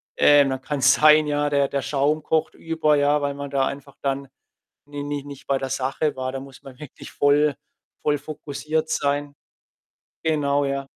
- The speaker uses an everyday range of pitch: No, narrow, 1.3 semitones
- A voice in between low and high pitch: Yes, medium, 145 Hz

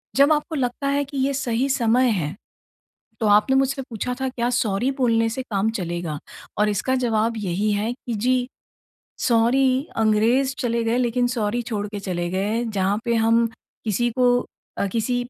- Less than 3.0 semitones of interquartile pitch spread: No, average, 3.3 semitones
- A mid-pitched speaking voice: No, high, 235 Hz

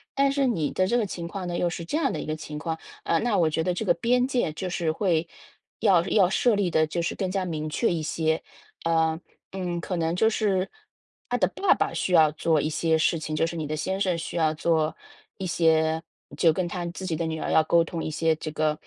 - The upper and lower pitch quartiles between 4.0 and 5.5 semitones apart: No, average, 2.9 semitones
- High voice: No, medium, 170 Hz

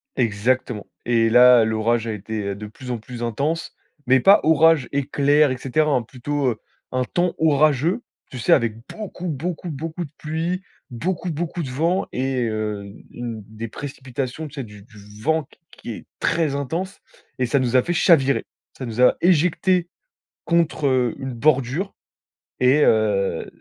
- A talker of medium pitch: No, low, 130 Hz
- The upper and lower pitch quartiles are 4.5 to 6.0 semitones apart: Yes, wide, 5.4 semitones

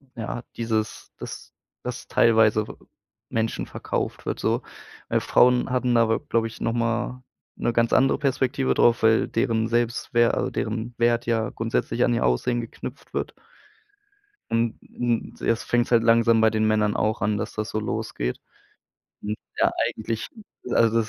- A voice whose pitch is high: No, low, 115 Hz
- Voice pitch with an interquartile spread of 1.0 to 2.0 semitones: Yes, narrow, 1.3 semitones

